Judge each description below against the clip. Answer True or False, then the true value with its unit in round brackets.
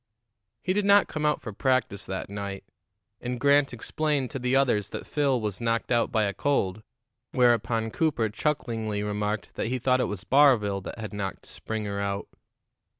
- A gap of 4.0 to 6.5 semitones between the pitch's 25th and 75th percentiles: True (4.7 semitones)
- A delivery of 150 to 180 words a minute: True (175 wpm)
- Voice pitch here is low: True (115 Hz)